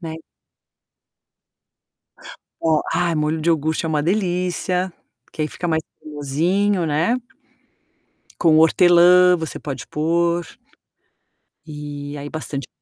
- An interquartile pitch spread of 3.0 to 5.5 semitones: No, narrow, 2.6 semitones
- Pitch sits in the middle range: Yes, medium, 160 Hz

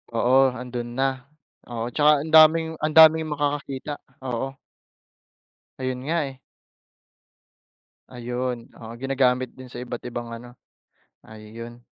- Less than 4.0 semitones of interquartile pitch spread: Yes, average, 3.3 semitones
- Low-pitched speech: Yes, low, 130 Hz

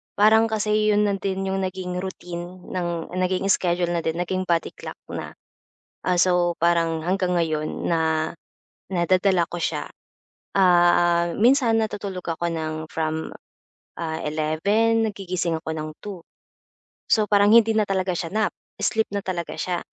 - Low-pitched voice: No, medium, 180 Hz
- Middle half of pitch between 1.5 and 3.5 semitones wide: Yes, average, 2.8 semitones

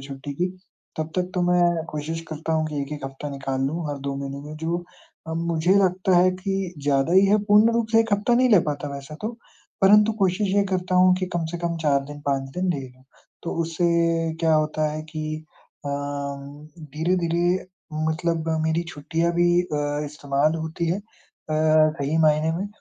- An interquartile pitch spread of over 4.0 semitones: No, average, 3.5 semitones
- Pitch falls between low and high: Yes, medium, 160 Hz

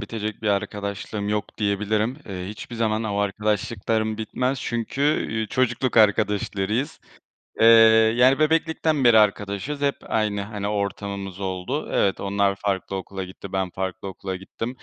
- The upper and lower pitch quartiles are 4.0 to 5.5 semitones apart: No, narrow, 2.5 semitones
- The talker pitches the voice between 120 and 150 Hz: No, low, 105 Hz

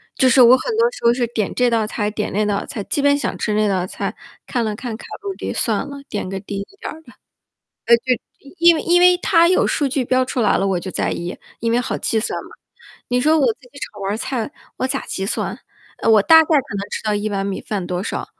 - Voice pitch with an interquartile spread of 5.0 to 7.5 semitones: Yes, wide, 5.4 semitones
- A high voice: Yes, high, 235 Hz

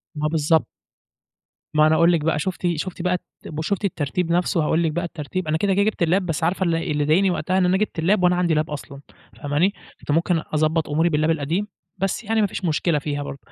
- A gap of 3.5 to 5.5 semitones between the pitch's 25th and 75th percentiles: No, average, 3.0 semitones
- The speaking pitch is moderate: Yes, medium, 165 Hz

